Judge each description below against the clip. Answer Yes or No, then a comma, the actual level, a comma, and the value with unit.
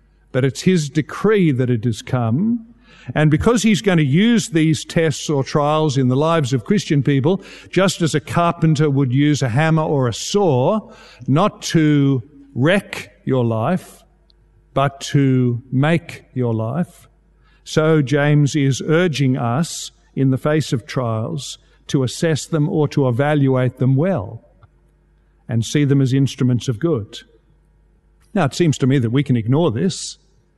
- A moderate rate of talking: Yes, average, 155 wpm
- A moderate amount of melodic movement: Yes, average, 4.0 semitones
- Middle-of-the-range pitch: Yes, medium, 145 Hz